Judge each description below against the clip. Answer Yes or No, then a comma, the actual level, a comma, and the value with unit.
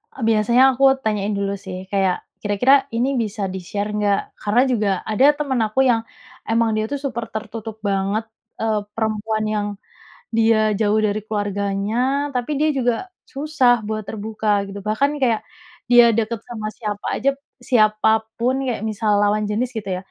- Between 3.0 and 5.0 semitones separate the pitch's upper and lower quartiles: No, narrow, 2.6 semitones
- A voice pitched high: Yes, high, 215 Hz